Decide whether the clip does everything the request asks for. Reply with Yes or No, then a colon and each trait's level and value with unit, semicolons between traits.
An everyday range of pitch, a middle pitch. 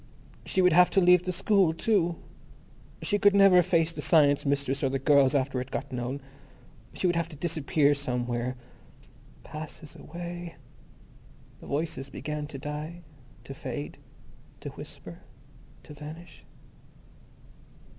Yes: average, 3.9 semitones; medium, 155 Hz